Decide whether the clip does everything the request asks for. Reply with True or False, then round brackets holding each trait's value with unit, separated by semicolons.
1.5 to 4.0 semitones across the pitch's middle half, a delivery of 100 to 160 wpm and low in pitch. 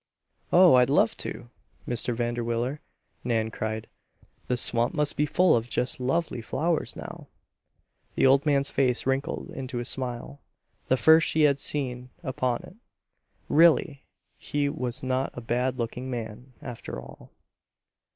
True (2.9 semitones; 140 wpm; 130 Hz)